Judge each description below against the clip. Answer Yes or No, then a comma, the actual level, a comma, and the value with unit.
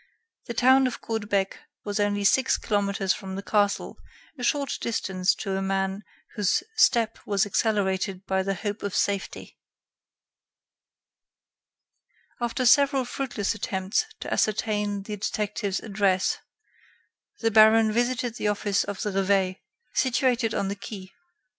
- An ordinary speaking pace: No, slow, 130 wpm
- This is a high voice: Yes, high, 205 Hz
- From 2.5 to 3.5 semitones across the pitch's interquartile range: Yes, average, 2.8 semitones